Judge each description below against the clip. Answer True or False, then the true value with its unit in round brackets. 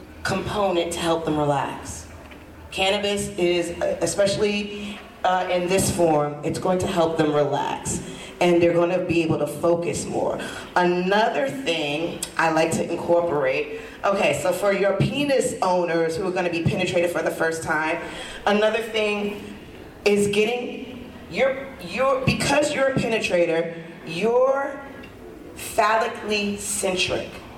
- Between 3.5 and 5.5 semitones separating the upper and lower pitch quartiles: True (4.4 semitones)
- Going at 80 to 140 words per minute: True (135 wpm)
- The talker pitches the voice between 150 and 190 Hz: True (185 Hz)